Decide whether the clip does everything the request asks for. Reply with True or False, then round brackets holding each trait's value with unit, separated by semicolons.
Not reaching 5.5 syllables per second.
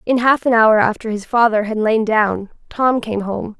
True (4.6 syllables/s)